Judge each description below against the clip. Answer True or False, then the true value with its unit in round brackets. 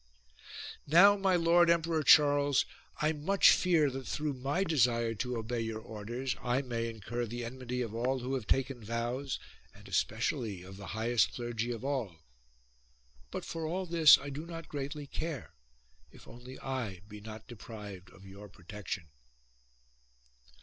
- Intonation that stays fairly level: False (4.7 semitones)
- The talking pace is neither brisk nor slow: True (160 wpm)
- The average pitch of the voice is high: False (125 Hz)